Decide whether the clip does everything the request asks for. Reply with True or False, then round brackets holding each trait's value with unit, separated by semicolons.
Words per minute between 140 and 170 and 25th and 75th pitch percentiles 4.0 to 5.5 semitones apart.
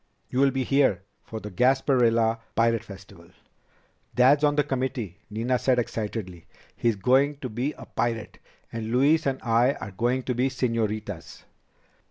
False (150 wpm; 3.3 semitones)